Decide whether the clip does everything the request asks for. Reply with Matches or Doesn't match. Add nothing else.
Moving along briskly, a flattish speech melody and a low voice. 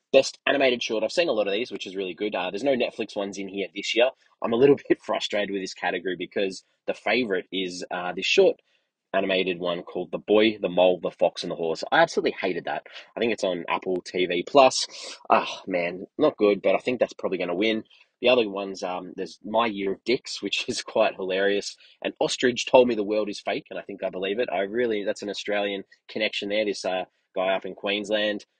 Matches